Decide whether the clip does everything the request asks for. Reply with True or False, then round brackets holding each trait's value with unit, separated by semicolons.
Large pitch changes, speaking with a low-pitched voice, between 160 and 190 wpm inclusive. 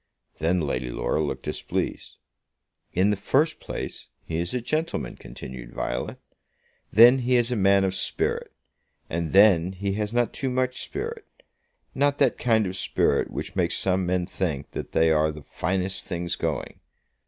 True (6.7 semitones; 95 Hz; 165 wpm)